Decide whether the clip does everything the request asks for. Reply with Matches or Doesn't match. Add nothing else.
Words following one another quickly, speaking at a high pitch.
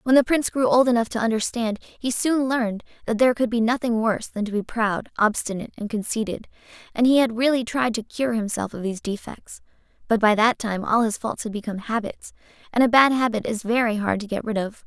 Matches